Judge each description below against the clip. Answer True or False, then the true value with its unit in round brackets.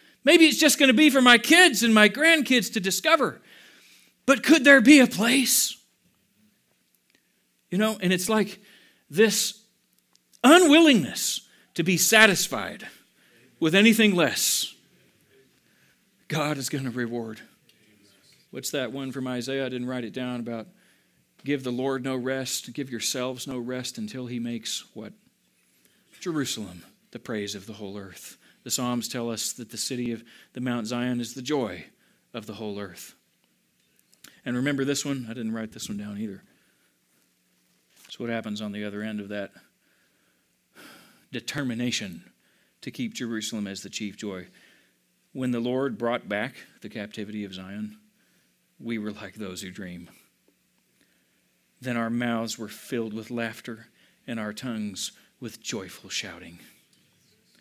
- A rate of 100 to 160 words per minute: True (150 wpm)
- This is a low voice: True (125 Hz)